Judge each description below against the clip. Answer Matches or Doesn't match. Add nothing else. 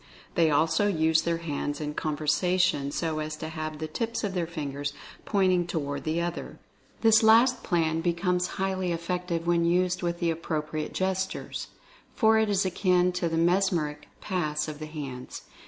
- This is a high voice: Doesn't match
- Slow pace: Doesn't match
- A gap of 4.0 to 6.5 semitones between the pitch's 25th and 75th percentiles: Doesn't match